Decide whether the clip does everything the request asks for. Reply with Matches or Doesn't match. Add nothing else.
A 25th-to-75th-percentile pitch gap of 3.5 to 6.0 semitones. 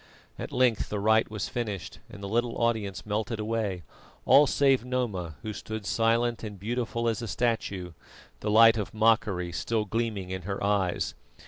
Doesn't match